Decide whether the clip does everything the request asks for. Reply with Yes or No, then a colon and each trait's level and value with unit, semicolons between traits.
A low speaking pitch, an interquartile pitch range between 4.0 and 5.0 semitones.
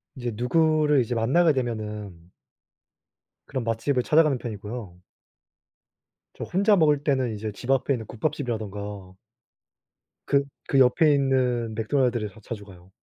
Yes: low, 120 Hz; average, 4.7 semitones